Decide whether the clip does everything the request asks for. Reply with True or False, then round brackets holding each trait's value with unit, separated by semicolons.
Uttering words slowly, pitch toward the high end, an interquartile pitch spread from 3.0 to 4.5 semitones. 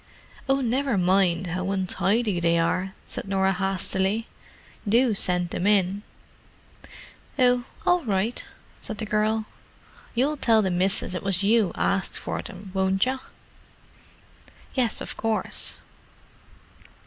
True (125 wpm; 195 Hz; 3.4 semitones)